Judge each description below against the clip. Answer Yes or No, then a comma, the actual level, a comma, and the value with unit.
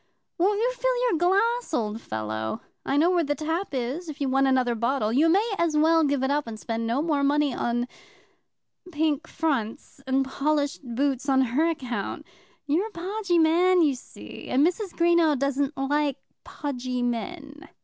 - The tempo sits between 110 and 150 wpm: No, average, 175 wpm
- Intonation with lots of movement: No, average, 4.6 semitones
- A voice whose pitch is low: No, very high, 290 Hz